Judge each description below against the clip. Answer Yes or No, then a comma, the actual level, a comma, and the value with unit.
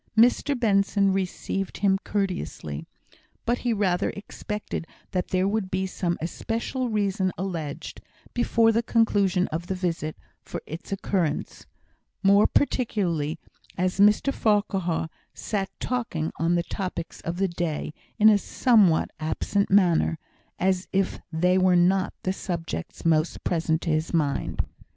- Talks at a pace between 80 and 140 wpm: Yes, slow, 135 wpm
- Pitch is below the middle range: No, high, 190 Hz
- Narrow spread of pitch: No, average, 3.3 semitones